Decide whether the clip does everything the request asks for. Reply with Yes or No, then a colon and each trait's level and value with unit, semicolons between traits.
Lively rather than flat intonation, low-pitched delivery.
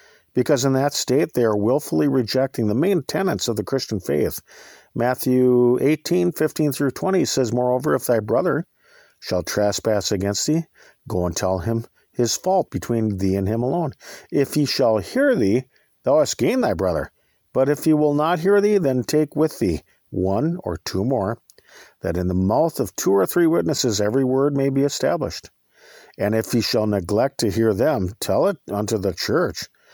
Yes: wide, 5.9 semitones; low, 125 Hz